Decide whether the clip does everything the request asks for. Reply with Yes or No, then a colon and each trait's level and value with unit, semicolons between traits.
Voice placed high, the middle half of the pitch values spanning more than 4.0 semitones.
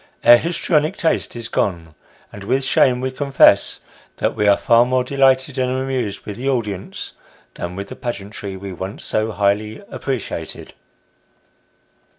No: low, 120 Hz; average, 4.7 semitones